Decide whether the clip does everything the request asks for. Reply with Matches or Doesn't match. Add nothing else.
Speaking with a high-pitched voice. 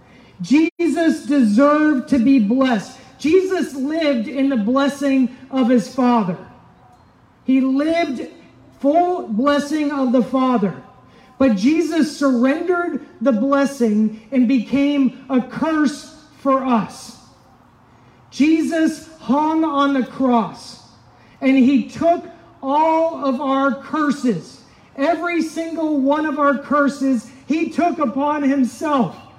Matches